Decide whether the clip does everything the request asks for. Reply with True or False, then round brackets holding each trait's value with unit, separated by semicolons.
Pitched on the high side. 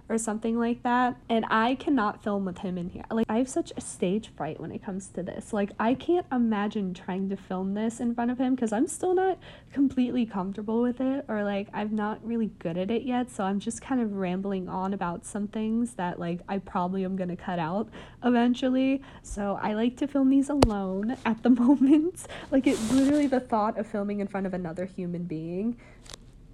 True (215 Hz)